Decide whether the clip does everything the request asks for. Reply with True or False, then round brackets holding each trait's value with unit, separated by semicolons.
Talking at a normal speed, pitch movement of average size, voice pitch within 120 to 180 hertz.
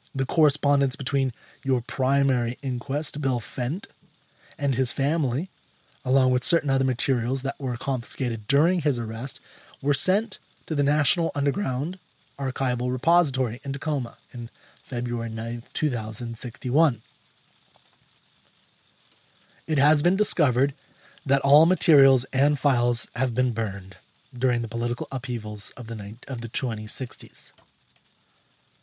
False (125 wpm; 3.0 semitones; 135 Hz)